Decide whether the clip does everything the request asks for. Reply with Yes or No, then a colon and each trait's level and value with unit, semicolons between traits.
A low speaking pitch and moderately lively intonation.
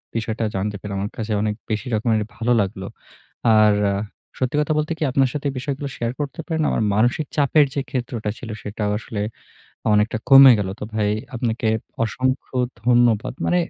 Yes: low, 115 Hz; average, 4.1 semitones